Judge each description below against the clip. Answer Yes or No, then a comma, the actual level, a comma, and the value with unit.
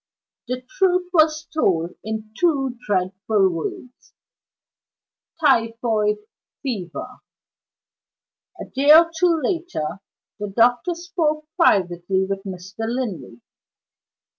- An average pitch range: No, wide, 8.2 semitones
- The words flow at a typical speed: No, slow, 90 wpm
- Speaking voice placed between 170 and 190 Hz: No, high, 230 Hz